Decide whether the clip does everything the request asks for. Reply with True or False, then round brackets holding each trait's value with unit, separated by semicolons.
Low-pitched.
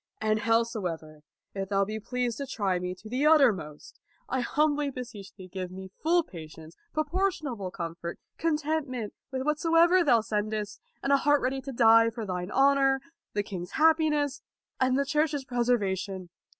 False (235 Hz)